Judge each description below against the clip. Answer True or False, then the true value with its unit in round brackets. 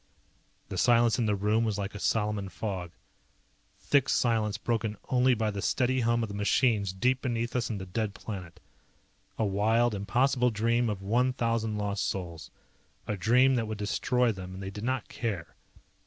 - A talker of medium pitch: False (110 Hz)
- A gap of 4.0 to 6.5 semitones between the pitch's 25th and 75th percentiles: False (3.0 semitones)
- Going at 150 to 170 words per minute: False (180 wpm)